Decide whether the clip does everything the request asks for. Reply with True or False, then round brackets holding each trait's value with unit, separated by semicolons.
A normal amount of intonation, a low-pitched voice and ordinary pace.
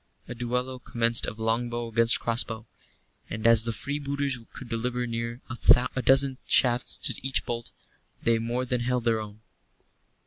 False (1.5 semitones; 120 Hz; 150 wpm)